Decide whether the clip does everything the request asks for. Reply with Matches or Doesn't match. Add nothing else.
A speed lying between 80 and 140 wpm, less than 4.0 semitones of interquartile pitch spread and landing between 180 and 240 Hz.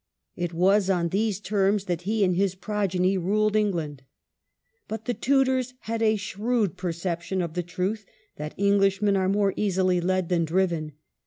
Doesn't match